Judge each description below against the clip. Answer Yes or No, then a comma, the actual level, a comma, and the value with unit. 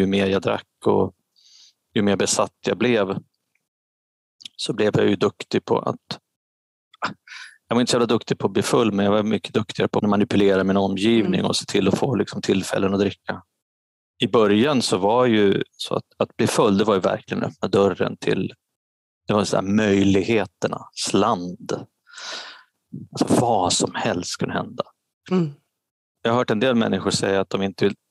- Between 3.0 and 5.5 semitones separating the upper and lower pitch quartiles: Yes, average, 3.3 semitones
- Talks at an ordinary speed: Yes, average, 185 wpm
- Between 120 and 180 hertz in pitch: No, low, 100 Hz